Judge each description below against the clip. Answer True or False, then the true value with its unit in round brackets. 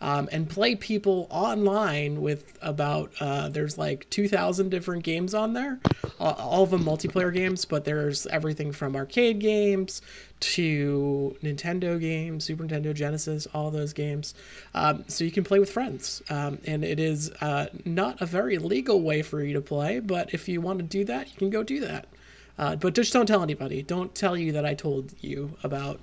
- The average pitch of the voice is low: False (160 Hz)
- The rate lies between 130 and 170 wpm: False (190 wpm)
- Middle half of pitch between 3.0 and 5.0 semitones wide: True (4.5 semitones)